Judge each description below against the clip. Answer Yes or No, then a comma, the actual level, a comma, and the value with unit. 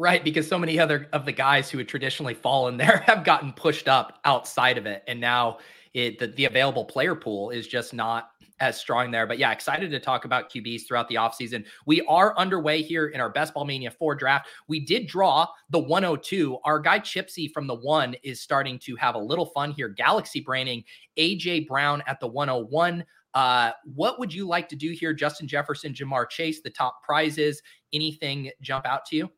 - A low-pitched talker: No, medium, 145 Hz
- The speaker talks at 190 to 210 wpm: Yes, fast, 205 wpm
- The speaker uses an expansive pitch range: No, average, 3.7 semitones